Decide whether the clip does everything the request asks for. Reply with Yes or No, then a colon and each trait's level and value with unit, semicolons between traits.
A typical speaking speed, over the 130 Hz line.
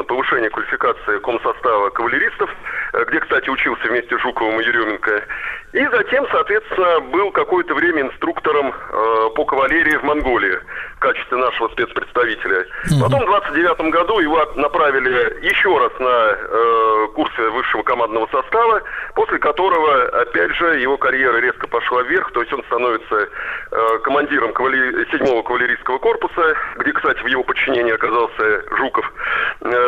Yes: average, 135 wpm; medium, 140 Hz